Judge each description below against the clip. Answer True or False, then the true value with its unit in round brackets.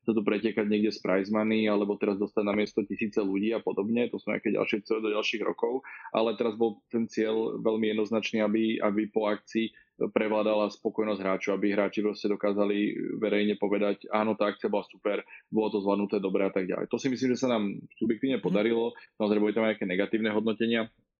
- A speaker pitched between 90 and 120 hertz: True (105 Hz)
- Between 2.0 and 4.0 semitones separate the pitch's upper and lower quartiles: False (1.4 semitones)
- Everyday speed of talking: False (205 wpm)